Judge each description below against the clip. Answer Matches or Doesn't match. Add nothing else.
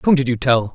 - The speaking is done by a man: Matches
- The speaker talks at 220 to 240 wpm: Doesn't match